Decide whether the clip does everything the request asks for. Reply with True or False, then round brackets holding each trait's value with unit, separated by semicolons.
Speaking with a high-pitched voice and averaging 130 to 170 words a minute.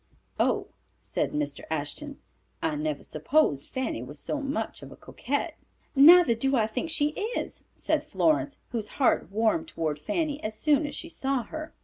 True (270 Hz; 165 wpm)